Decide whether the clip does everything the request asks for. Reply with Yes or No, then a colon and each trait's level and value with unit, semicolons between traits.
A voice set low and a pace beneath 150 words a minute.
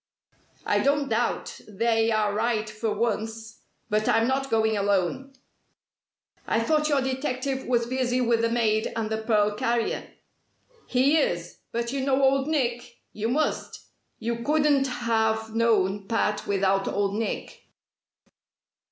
No: high, 230 Hz; slow, 135 wpm